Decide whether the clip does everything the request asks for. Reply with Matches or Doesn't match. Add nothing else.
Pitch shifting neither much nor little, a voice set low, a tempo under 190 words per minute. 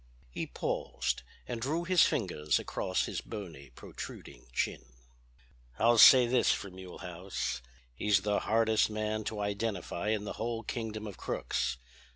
Matches